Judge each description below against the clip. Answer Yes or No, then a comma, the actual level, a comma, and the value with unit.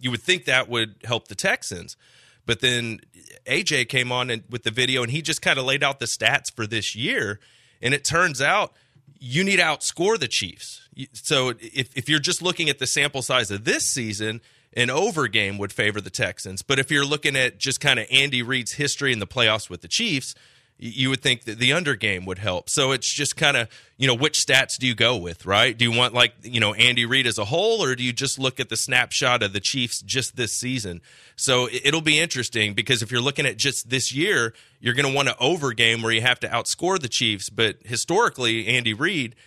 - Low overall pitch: Yes, low, 125 Hz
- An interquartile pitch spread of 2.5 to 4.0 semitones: Yes, average, 3.4 semitones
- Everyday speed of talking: No, fast, 235 wpm